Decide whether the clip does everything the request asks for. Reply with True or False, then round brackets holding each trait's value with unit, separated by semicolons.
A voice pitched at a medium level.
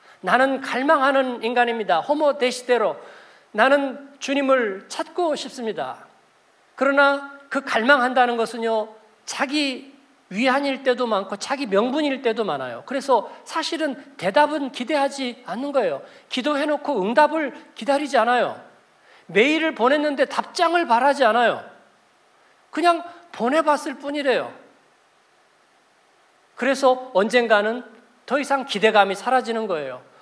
False (270 Hz)